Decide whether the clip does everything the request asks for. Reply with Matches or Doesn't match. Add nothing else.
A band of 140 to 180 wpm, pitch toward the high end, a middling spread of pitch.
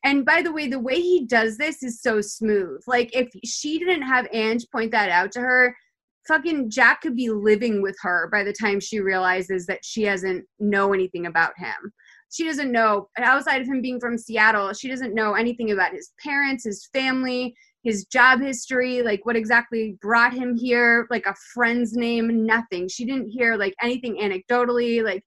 Doesn't match